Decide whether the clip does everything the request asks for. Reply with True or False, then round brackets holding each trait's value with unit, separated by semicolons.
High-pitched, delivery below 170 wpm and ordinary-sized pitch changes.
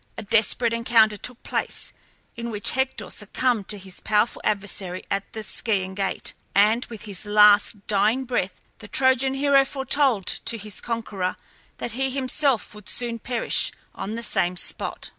True (220 Hz; 160 wpm; 3.4 semitones)